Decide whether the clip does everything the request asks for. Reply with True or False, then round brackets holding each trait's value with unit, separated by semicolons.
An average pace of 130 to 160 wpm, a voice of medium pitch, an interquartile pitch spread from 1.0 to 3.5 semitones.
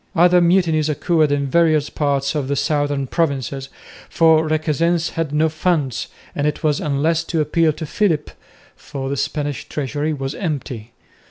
True (155 wpm; 150 Hz; 2.5 semitones)